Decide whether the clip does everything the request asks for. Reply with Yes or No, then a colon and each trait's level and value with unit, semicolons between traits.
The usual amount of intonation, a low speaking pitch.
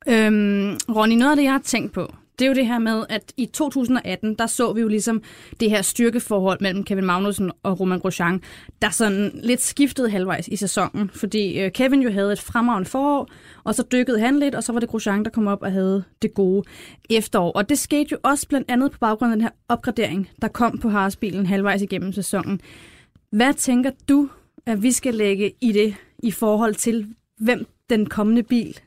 No: average, 3.5 semitones; high, 220 Hz